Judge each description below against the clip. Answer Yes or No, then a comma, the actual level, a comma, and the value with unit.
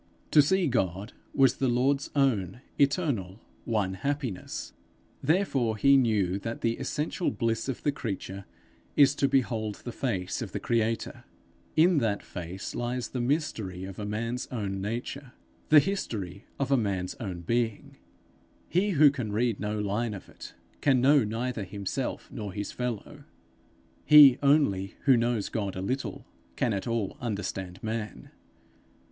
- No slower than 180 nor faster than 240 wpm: No, average, 150 wpm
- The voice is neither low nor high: No, low, 115 Hz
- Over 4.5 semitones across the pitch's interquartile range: Yes, average, 5.2 semitones